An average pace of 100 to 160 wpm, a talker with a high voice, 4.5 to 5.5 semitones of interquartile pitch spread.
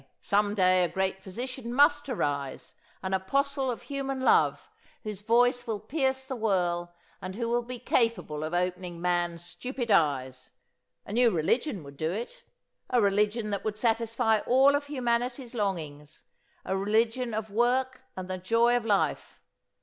Yes: average, 155 wpm; high, 220 Hz; average, 5.1 semitones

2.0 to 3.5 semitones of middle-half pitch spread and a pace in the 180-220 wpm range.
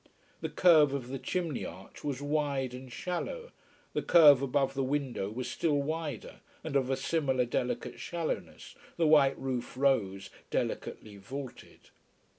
No: average, 3.1 semitones; average, 145 wpm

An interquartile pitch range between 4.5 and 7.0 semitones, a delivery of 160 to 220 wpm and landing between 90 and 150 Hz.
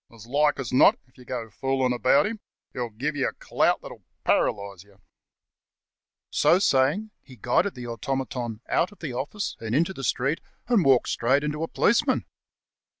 No: average, 4.0 semitones; average, 175 wpm; low, 135 Hz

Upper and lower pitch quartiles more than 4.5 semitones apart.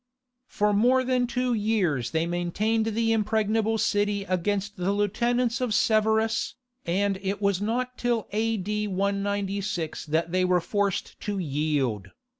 No: average, 3.2 semitones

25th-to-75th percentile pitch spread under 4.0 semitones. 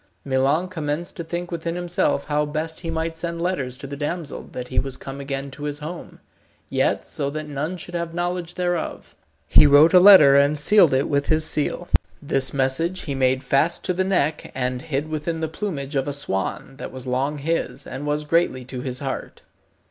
Yes: average, 3.6 semitones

